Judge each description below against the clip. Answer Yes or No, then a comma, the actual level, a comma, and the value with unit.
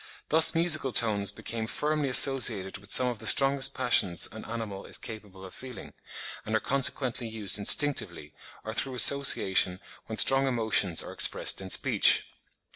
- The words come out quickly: No, average, 155 wpm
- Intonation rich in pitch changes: No, average, 5.0 semitones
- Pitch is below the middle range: Yes, low, 115 Hz